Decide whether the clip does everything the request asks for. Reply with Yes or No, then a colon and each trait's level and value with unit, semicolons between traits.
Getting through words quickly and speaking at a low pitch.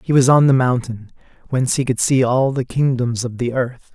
Yes: fast, 230 wpm; low, 125 Hz